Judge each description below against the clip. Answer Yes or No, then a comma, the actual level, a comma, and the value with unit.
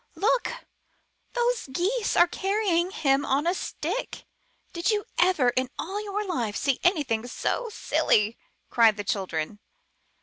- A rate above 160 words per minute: No, average, 140 wpm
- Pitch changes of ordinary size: No, wide, 8.8 semitones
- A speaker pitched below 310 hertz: No, very high, 340 Hz